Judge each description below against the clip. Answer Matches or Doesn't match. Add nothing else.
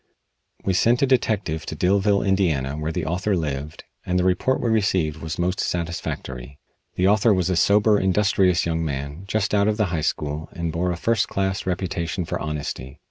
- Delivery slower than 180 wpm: Doesn't match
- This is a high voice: Doesn't match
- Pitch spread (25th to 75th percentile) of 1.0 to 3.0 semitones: Doesn't match